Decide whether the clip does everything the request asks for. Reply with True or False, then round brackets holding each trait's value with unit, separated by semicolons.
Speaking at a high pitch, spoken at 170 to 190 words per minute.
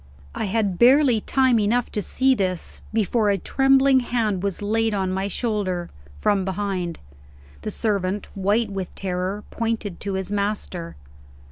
False (205 Hz; 145 wpm)